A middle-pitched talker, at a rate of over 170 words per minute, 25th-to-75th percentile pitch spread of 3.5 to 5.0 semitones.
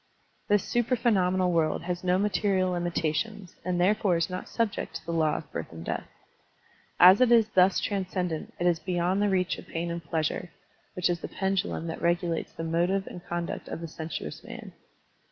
No: medium, 180 Hz; average, 190 wpm; narrow, 2.4 semitones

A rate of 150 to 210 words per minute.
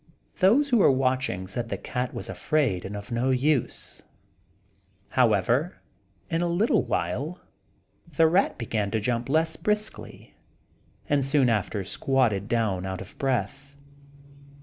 No: slow, 135 wpm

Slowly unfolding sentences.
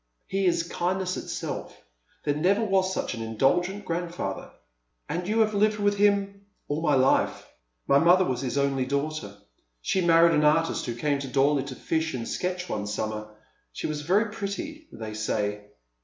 No: average, 185 wpm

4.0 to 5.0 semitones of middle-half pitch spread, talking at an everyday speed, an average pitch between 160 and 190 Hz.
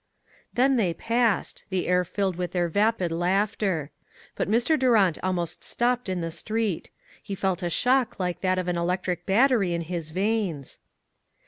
Yes: average, 4.3 semitones; average, 160 wpm; medium, 185 Hz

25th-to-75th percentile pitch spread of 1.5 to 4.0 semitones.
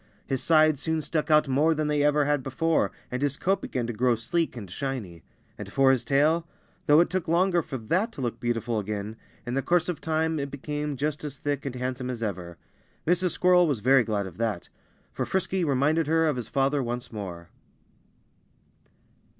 No: average, 4.9 semitones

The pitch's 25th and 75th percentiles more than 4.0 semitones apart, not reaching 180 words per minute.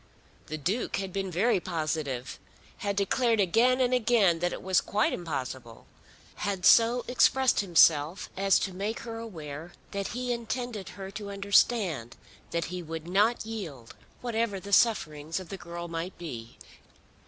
Yes: average, 5.2 semitones; average, 155 wpm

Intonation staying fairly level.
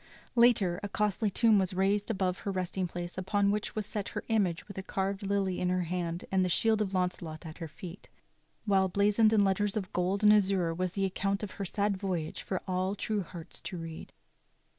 Yes: narrow, 2.1 semitones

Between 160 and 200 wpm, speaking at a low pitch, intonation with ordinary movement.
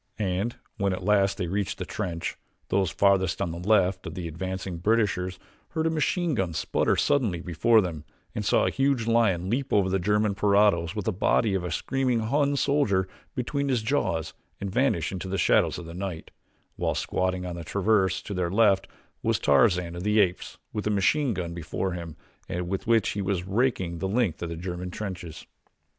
Yes: average, 195 wpm; very low, 95 Hz; average, 3.8 semitones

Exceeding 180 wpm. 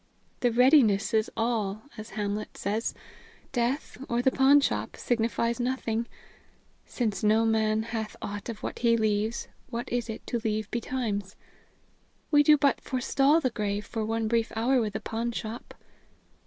No: average, 150 wpm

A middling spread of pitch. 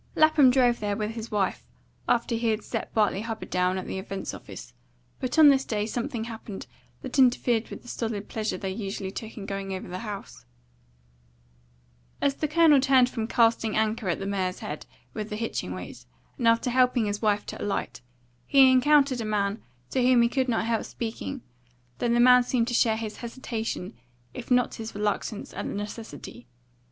Yes: average, 3.3 semitones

